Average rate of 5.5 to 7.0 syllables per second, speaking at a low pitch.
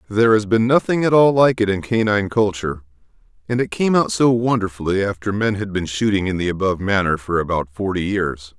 Yes: 6.0 syllables/s; low, 100 Hz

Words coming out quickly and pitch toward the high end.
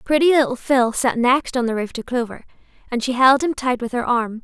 Yes: fast, 245 wpm; very high, 250 Hz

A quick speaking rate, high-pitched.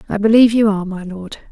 Yes: fast, 240 wpm; high, 205 Hz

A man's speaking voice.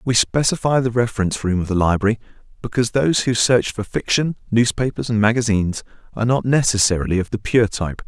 Yes: male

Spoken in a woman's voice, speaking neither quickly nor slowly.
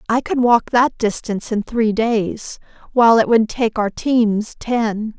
Yes: female; average, 175 wpm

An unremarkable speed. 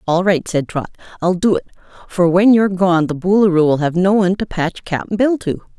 No: fast, 230 wpm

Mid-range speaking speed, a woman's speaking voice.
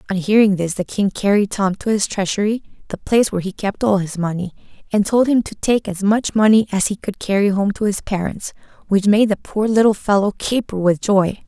No: fast, 225 wpm; female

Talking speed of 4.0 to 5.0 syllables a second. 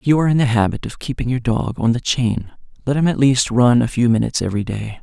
No: 6.4 syllables/s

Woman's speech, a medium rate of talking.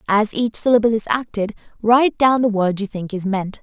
No: female; fast, 215 wpm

